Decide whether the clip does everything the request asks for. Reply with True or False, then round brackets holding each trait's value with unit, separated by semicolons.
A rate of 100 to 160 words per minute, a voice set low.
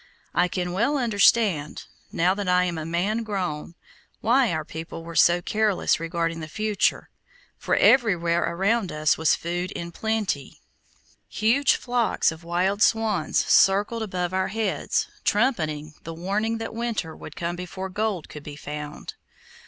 False (150 wpm; 180 Hz)